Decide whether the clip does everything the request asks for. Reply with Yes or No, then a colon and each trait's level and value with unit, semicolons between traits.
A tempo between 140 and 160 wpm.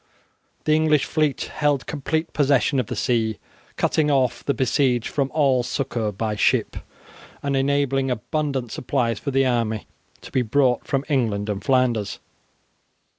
Yes: average, 145 wpm